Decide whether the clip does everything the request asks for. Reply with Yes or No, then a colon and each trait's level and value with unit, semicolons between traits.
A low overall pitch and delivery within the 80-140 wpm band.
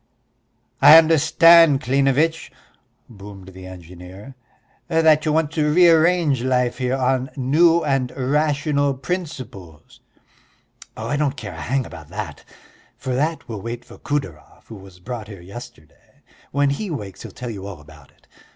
No: low, 130 Hz; average, 150 wpm